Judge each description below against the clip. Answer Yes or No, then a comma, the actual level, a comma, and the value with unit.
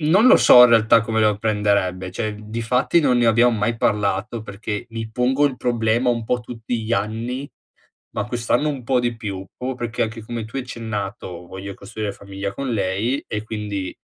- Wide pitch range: No, average, 2.8 semitones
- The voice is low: Yes, low, 115 Hz